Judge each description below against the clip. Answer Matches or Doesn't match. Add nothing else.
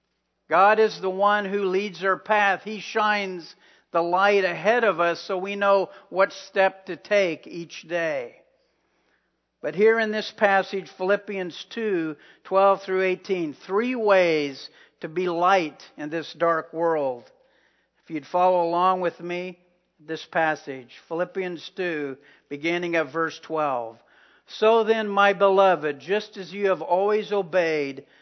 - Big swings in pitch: Doesn't match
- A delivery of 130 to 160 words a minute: Matches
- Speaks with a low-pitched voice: Doesn't match